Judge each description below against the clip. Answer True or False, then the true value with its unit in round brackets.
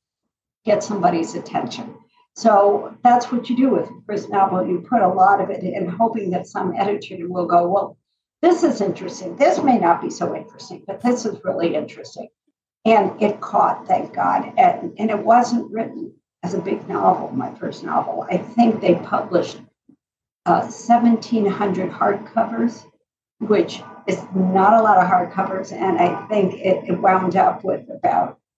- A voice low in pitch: False (205 Hz)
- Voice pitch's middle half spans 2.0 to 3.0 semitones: False (3.8 semitones)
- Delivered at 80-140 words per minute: False (170 wpm)